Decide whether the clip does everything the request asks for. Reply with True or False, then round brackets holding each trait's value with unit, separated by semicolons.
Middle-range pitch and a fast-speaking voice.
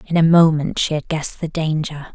True (155 Hz; 225 wpm)